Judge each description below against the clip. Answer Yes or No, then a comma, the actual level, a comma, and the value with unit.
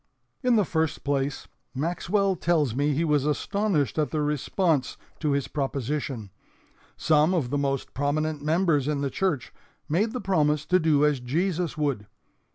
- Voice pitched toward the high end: No, medium, 150 Hz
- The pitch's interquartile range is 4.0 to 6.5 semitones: No, average, 3.3 semitones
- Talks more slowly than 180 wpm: Yes, average, 160 wpm